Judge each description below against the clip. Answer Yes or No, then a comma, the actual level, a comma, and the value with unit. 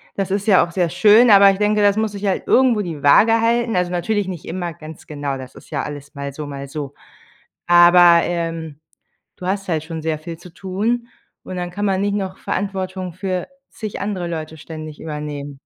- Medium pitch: Yes, medium, 180 Hz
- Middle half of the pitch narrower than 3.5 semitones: No, average, 4.3 semitones